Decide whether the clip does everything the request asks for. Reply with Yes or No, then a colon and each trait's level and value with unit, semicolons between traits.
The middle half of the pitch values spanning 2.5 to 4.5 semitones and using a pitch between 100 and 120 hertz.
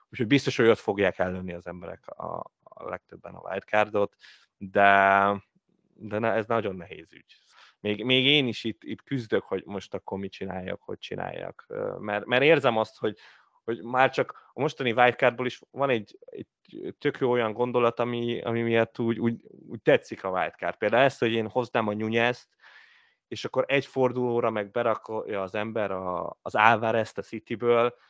Yes: average, 3.0 semitones; low, 115 Hz